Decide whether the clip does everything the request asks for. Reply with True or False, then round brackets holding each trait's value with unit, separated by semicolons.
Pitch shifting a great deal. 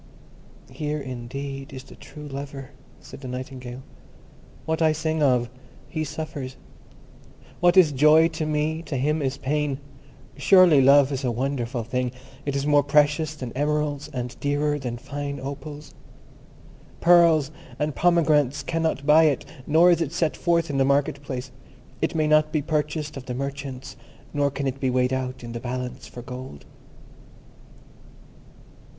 False (2.7 semitones)